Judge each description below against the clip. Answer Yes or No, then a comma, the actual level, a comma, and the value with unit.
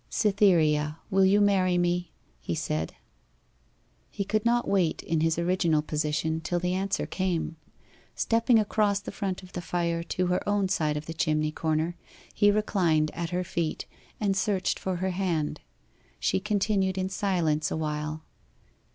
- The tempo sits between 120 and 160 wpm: Yes, average, 155 wpm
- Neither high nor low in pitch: Yes, medium, 180 Hz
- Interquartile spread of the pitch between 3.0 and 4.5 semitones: Yes, average, 3.6 semitones